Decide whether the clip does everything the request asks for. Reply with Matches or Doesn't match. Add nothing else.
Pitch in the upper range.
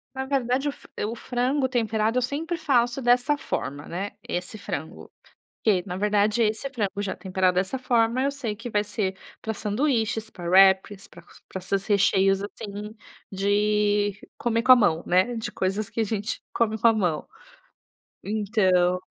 Matches